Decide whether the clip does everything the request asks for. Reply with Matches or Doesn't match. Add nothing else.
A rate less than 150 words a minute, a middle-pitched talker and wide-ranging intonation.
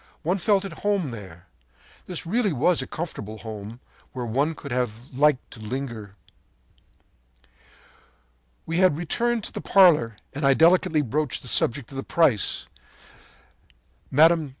Matches